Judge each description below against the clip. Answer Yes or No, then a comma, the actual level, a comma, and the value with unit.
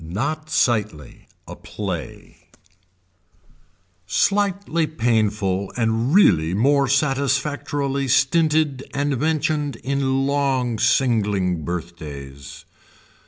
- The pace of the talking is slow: Yes, slow, 75 wpm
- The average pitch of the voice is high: No, low, 135 Hz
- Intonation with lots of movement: Yes, wide, 6.3 semitones